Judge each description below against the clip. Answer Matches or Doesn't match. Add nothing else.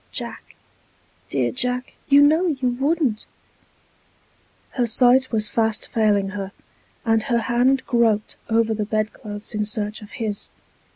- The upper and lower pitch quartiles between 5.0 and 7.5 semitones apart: Doesn't match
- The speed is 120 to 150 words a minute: Matches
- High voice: Matches